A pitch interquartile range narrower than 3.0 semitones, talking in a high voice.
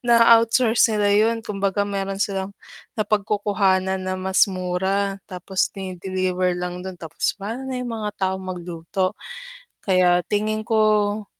Yes: narrow, 2.4 semitones; high, 195 Hz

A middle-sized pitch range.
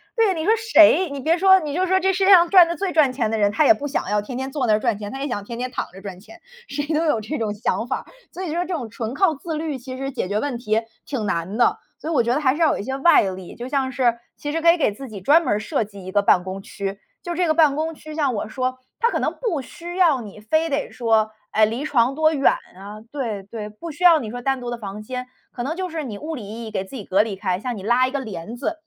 No: wide, 6.7 semitones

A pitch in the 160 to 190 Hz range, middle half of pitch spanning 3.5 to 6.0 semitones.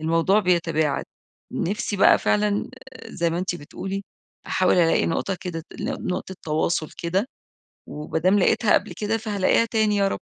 Yes: medium, 185 Hz; average, 3.8 semitones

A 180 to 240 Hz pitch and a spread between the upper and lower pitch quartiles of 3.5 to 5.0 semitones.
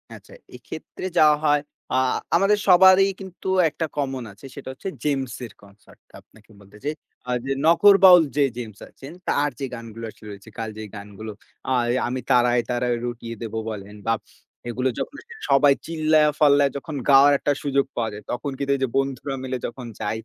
No: low, 135 Hz; average, 4.3 semitones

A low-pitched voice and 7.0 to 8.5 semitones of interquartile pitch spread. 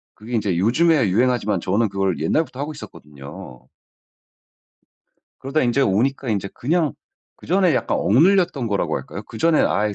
Yes: low, 120 Hz; wide, 7.4 semitones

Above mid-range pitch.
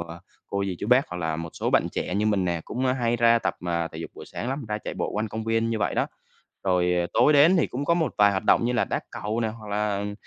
No: low, 105 Hz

